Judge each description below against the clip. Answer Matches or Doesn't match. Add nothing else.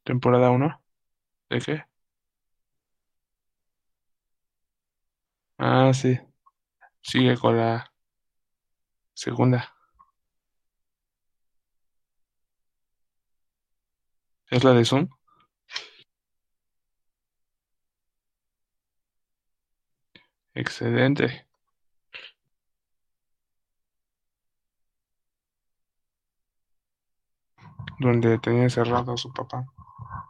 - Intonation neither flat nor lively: Doesn't match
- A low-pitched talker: Matches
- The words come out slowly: Matches